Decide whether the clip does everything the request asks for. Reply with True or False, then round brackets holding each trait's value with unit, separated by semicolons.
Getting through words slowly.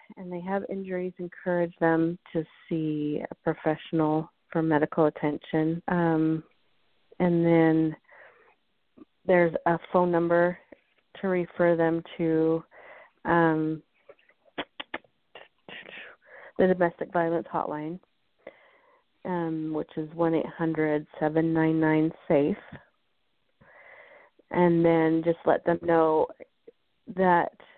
True (95 wpm)